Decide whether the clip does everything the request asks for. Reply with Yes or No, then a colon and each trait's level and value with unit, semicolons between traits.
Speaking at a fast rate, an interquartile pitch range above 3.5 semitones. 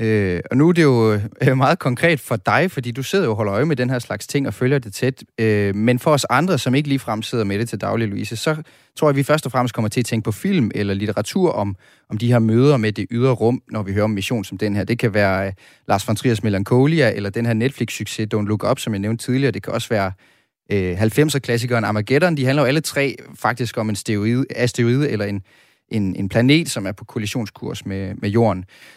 Yes: fast, 250 wpm; average, 3.9 semitones